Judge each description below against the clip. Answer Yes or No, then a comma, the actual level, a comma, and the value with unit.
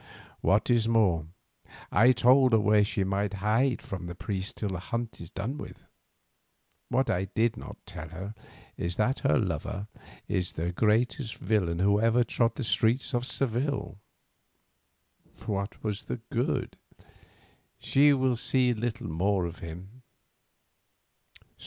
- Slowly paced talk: No, average, 145 wpm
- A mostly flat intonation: No, average, 4.2 semitones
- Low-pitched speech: Yes, low, 110 Hz